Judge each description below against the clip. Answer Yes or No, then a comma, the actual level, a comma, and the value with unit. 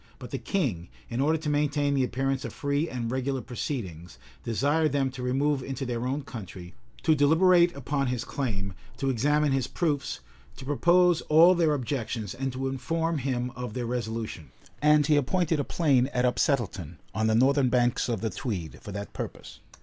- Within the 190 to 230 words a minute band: No, average, 180 wpm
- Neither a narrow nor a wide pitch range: Yes, average, 3.6 semitones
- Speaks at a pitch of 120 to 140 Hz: Yes, low, 135 Hz